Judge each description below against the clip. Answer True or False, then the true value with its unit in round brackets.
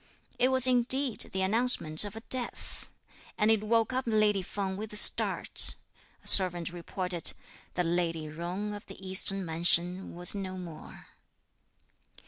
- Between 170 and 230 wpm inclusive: False (145 wpm)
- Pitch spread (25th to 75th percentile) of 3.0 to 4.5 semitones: True (3.8 semitones)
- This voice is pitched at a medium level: False (195 Hz)